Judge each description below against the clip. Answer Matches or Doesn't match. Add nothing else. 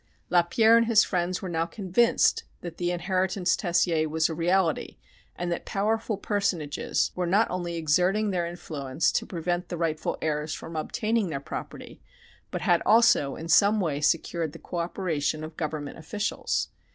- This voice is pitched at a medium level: Matches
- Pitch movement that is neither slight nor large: Matches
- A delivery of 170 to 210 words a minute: Doesn't match